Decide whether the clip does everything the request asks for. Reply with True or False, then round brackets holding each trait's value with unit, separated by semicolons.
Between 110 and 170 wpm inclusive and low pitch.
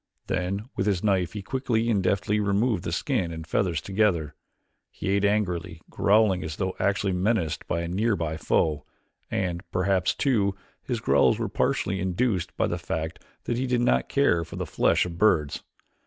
False (180 wpm; 95 Hz)